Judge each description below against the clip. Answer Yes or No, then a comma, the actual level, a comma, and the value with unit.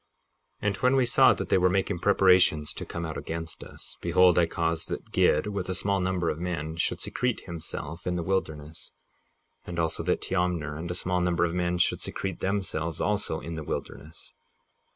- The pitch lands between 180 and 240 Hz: No, very low, 90 Hz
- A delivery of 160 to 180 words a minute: No, average, 195 wpm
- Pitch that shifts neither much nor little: No, narrow, 2.3 semitones